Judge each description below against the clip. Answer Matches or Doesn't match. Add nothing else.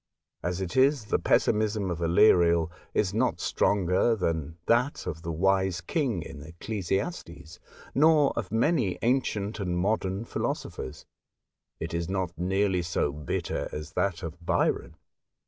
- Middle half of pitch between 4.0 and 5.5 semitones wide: Matches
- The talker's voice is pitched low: Matches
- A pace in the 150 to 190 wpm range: Doesn't match